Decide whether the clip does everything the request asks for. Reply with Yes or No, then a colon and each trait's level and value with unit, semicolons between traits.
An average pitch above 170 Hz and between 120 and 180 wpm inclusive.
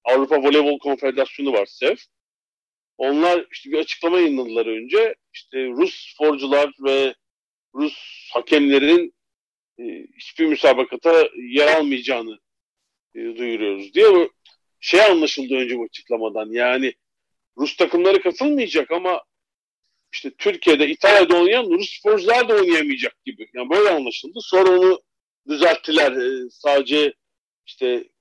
No: medium, 185 Hz; average, 105 wpm